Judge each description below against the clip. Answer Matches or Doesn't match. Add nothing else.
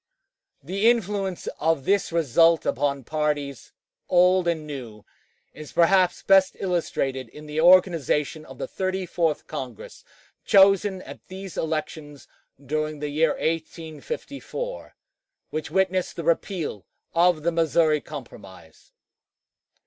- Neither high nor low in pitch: Matches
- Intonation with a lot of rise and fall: Doesn't match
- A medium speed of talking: Doesn't match